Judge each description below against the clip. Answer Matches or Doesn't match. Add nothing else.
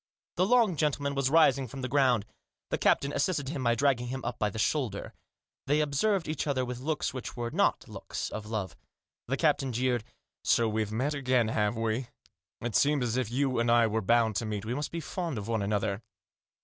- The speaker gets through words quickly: Matches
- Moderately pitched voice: Doesn't match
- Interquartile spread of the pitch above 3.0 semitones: Matches